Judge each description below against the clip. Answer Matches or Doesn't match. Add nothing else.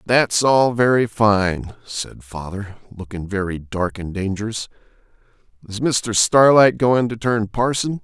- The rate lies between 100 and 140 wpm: Matches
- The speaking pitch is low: Matches